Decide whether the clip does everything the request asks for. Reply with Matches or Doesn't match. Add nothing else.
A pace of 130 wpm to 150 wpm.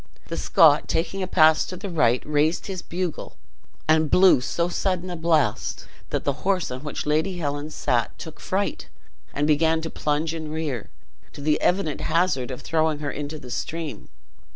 Doesn't match